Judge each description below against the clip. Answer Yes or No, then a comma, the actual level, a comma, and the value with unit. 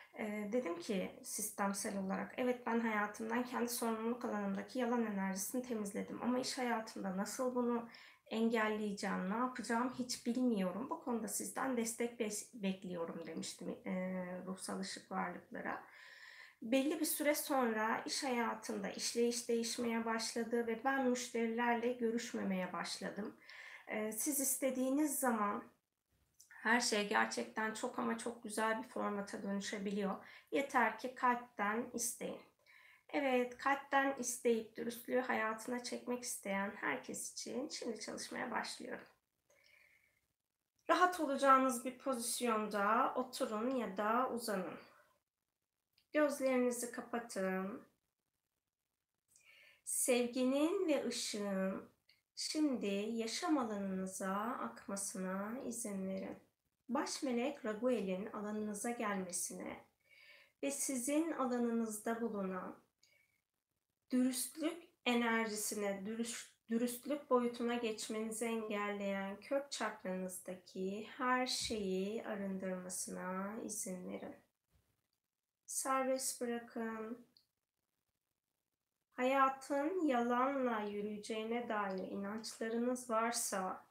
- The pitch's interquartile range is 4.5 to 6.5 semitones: No, average, 3.4 semitones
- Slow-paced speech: Yes, slow, 90 wpm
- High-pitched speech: Yes, high, 235 Hz